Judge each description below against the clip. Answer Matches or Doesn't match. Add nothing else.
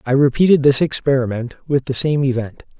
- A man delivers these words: Matches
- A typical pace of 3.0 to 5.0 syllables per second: Doesn't match